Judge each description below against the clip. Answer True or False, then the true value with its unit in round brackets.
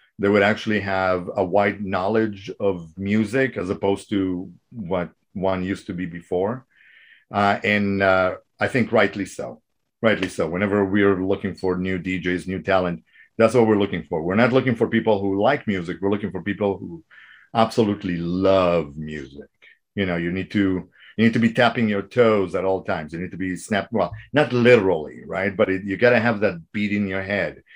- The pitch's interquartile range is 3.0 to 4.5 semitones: False (2.4 semitones)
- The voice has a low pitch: True (100 Hz)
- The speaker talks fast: False (195 wpm)